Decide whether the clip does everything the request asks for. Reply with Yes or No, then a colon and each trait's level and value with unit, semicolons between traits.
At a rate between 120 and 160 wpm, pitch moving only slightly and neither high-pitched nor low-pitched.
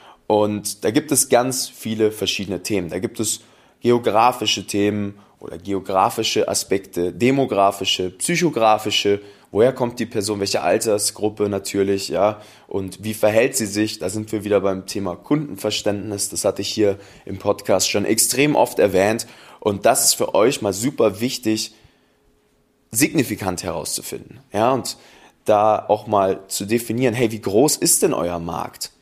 No: average, 150 wpm; narrow, 2.2 semitones; low, 105 Hz